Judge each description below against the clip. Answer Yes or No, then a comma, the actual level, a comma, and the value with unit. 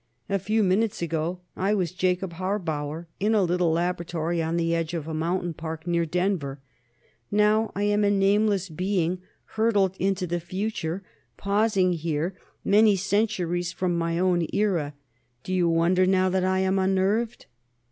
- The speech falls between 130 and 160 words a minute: Yes, average, 155 wpm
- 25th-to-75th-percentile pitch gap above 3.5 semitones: No, average, 2.8 semitones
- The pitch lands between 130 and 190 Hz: Yes, medium, 185 Hz